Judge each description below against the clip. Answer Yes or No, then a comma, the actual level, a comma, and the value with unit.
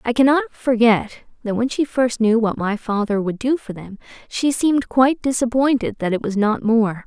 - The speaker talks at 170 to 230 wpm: Yes, fast, 205 wpm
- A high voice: Yes, high, 235 Hz